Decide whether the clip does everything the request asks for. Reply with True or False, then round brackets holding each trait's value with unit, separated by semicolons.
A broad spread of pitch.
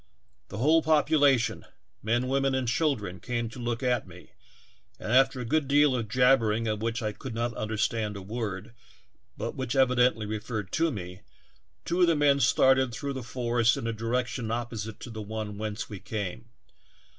False (3.4 semitones)